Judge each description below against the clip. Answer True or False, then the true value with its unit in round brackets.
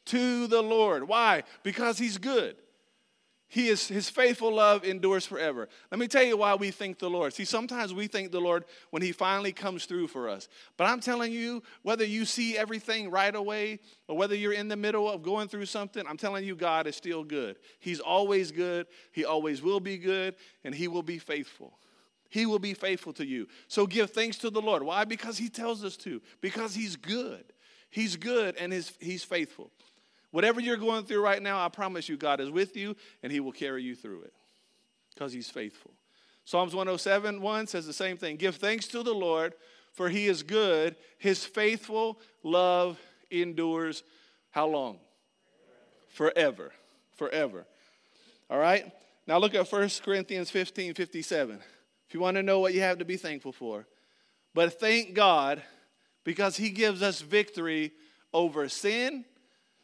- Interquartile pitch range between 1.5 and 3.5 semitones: False (4.0 semitones)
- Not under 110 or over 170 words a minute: False (180 wpm)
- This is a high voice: True (195 Hz)